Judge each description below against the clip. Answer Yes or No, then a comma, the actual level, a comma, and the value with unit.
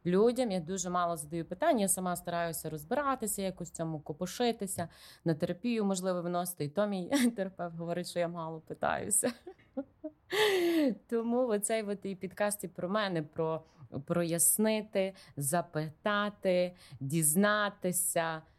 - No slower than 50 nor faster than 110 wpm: No, average, 120 wpm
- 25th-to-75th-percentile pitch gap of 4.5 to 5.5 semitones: No, average, 3.7 semitones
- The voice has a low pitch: No, medium, 180 Hz